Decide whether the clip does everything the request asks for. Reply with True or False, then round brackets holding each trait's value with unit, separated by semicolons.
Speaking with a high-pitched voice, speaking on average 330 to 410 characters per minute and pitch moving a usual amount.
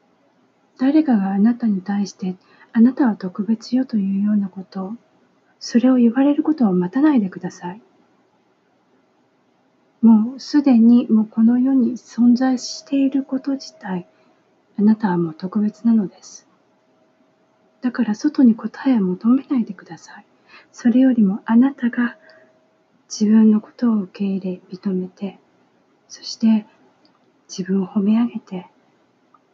False (225 Hz; 260 characters per minute; 4.1 semitones)